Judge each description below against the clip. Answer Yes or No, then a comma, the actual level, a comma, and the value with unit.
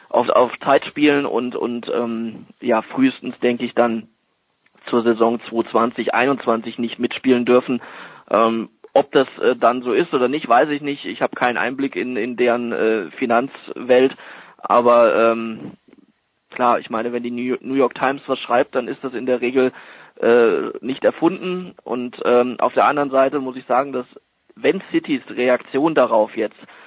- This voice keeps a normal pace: Yes, average, 175 wpm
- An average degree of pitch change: No, narrow, 2.3 semitones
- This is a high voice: No, low, 125 Hz